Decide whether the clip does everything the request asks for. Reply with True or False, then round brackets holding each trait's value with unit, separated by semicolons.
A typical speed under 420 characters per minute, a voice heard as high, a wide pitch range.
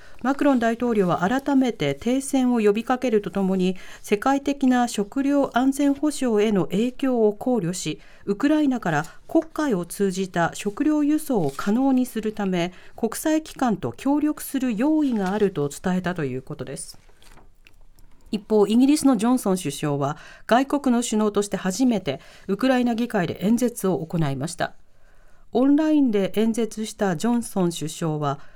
True (315 characters per minute; 220 Hz; 6.0 semitones)